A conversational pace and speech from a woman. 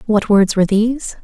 Yes: average, 195 wpm; female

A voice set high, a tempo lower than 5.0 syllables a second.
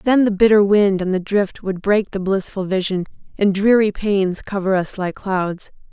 Yes: high, 195 Hz; 4.5 syllables/s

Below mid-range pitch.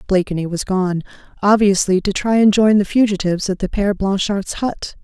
No: high, 195 Hz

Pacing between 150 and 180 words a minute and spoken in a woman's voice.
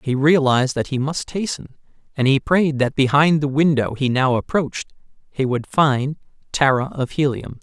No: average, 175 wpm; male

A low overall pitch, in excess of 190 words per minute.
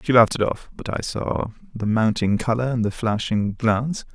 Yes: low, 115 Hz; fast, 205 wpm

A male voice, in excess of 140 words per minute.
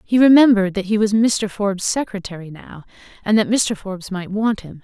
No: female; average, 200 wpm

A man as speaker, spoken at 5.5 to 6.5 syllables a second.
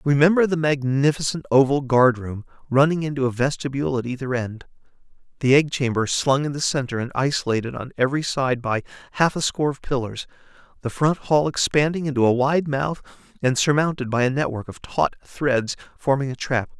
Yes: male; 5.6 syllables/s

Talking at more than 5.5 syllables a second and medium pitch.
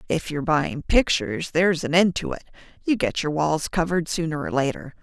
Yes: 5.7 syllables/s; medium, 160 Hz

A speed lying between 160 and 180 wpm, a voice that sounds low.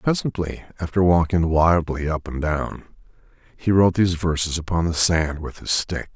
Yes: average, 165 wpm; very low, 85 Hz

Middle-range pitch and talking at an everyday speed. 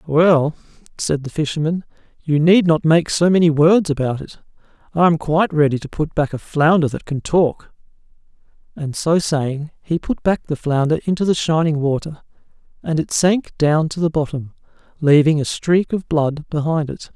Yes: medium, 155 Hz; average, 180 wpm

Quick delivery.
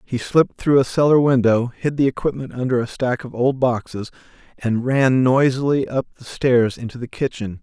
No: average, 190 wpm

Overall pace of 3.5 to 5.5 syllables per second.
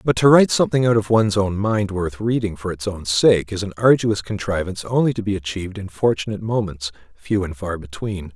No: 5.9 syllables/s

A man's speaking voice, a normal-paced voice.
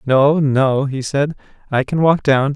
Yes: male; average, 190 wpm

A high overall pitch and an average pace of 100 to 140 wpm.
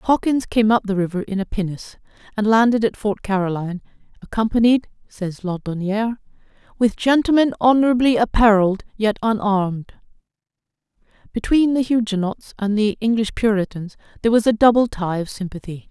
Yes: high, 215 Hz; slow, 135 wpm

